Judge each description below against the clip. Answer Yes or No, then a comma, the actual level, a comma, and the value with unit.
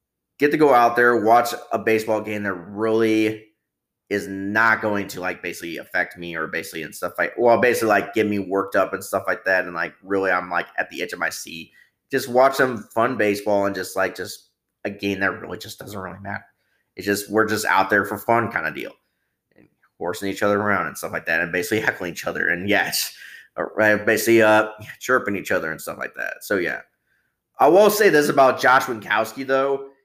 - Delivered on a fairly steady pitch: Yes, narrow, 2.3 semitones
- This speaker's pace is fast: Yes, fast, 220 wpm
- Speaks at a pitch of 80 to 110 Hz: Yes, low, 105 Hz